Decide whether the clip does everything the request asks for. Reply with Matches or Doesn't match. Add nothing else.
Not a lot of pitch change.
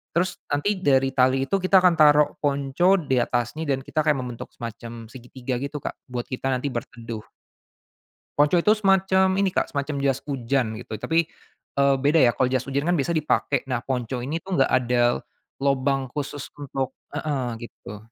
Doesn't match